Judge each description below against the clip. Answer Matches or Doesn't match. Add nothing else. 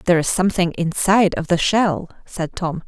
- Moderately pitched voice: Matches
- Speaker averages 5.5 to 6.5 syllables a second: Doesn't match